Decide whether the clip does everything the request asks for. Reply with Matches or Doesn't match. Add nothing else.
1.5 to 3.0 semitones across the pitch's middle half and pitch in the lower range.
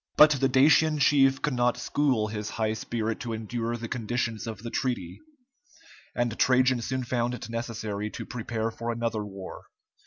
Matches